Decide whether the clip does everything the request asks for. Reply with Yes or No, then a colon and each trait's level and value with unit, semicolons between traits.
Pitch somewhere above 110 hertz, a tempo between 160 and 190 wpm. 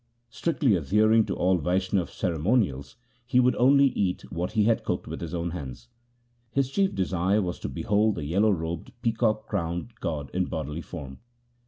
No: very low, 95 Hz; average, 170 wpm